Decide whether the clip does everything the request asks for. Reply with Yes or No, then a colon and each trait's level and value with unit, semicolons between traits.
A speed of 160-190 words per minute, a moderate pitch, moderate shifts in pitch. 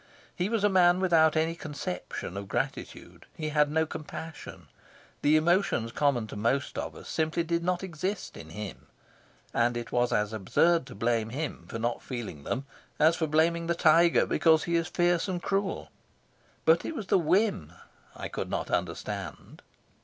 No: average, 175 wpm; medium, 160 Hz; wide, 6.3 semitones